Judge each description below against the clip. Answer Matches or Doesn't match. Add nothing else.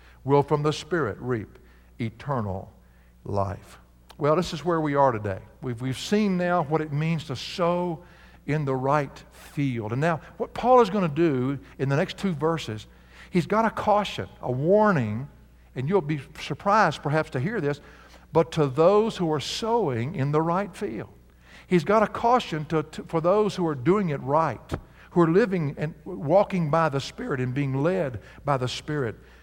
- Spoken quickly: Doesn't match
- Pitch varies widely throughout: Matches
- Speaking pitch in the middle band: Matches